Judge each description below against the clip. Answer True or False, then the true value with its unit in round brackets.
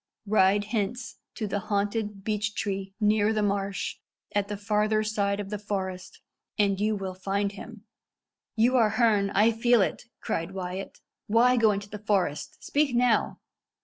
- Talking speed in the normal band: True (155 wpm)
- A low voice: False (205 Hz)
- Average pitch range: False (1.7 semitones)